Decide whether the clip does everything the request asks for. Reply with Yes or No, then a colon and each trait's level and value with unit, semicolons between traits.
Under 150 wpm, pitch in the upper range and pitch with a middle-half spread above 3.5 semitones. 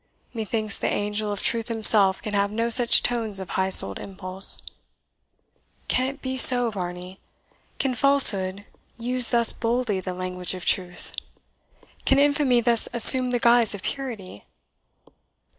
Yes: average, 140 wpm; high, 220 Hz; average, 4.3 semitones